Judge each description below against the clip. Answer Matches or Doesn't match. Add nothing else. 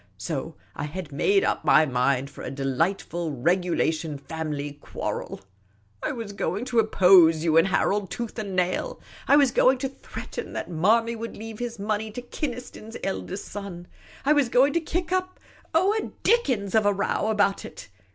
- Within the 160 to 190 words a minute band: Matches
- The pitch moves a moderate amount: Doesn't match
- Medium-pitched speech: Doesn't match